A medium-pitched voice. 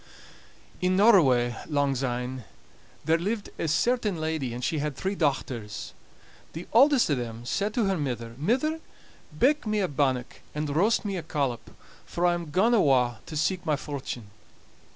Yes: medium, 155 Hz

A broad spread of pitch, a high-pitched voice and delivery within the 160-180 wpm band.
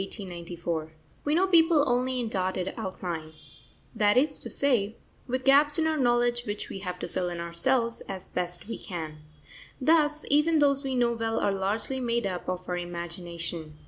Yes: wide, 7.0 semitones; high, 220 Hz; average, 175 wpm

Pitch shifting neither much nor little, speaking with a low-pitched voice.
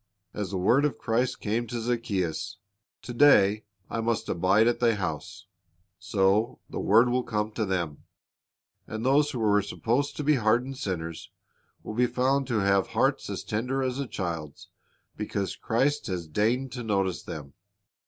Yes: average, 4.3 semitones; low, 110 Hz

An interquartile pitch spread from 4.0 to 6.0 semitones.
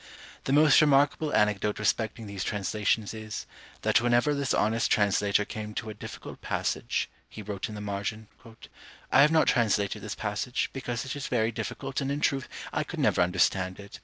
Yes: average, 4.3 semitones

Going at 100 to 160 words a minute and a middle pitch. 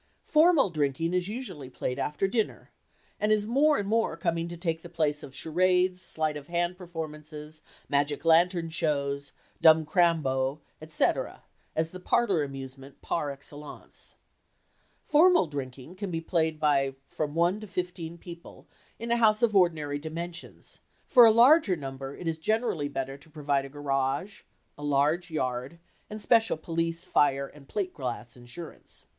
Yes: average, 155 wpm; medium, 160 Hz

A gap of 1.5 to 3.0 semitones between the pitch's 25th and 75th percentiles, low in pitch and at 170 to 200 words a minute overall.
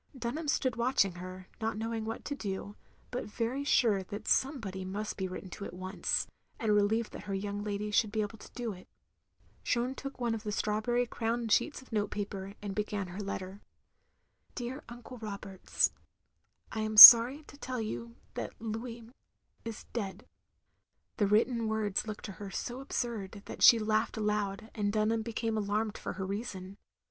No: narrow, 2.5 semitones; high, 215 Hz; average, 180 wpm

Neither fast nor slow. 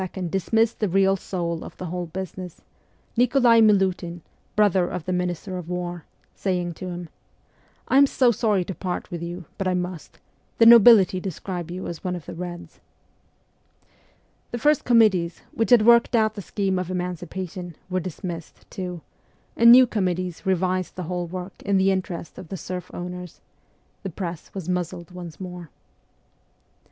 Yes: average, 165 wpm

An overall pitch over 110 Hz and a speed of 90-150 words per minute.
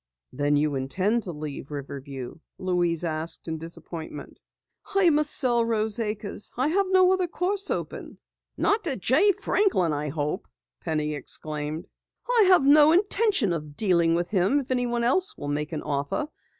No: medium, 185 Hz; average, 160 wpm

